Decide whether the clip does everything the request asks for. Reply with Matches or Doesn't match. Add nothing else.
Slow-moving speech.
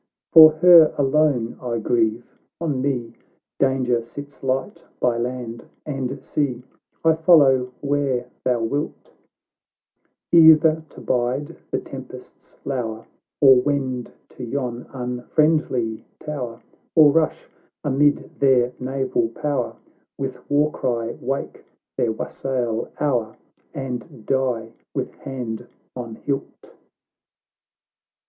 Matches